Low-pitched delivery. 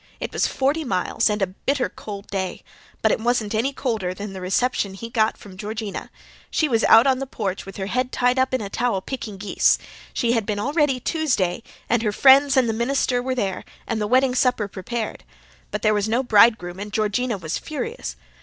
No: high, 225 Hz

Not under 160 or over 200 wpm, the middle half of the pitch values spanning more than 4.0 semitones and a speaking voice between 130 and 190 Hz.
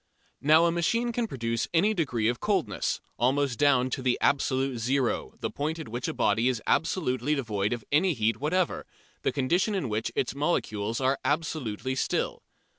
Yes: average, 175 wpm; average, 5.1 semitones; low, 135 Hz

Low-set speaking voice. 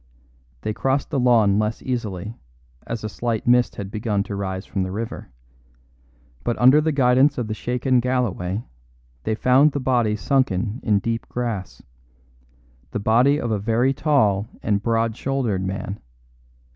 Yes: low, 115 Hz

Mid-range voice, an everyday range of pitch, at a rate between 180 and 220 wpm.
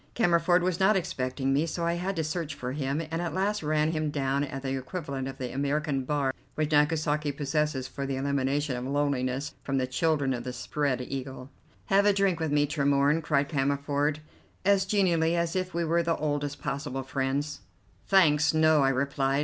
Yes: medium, 145 Hz; average, 3.2 semitones; average, 190 wpm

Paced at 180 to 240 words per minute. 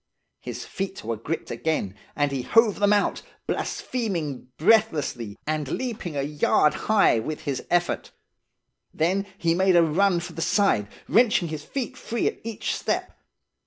No: average, 155 wpm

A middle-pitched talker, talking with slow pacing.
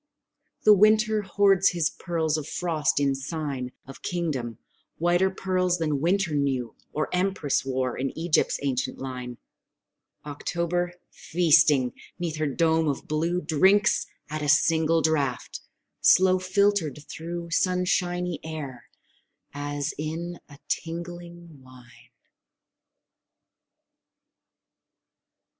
Yes: medium, 160 Hz; slow, 105 wpm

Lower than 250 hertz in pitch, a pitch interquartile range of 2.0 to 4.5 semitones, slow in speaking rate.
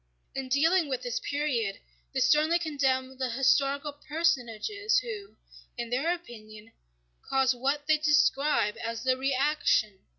No: very high, 275 Hz; average, 3.8 semitones; slow, 130 wpm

